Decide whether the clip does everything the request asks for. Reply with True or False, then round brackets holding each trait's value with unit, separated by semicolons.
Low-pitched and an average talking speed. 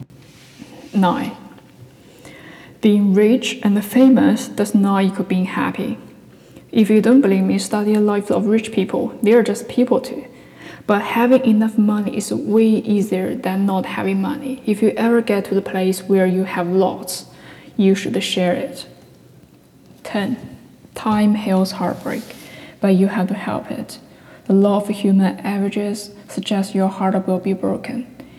False (205 Hz; 155 wpm)